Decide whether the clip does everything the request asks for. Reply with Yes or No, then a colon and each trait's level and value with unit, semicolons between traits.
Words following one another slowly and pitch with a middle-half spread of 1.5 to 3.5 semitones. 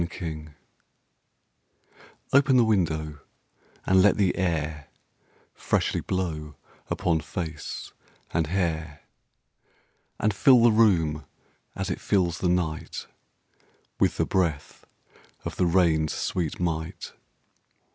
Yes: slow, 105 wpm; average, 3.2 semitones